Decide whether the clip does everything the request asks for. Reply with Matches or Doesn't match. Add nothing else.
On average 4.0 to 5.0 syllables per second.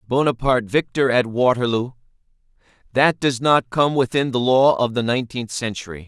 Doesn't match